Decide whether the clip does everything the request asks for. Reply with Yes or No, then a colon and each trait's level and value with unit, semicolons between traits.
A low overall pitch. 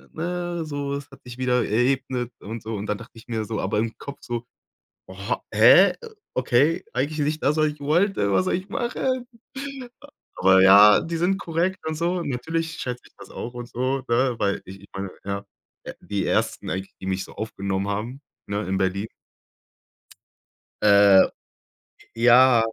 Yes: low, 125 Hz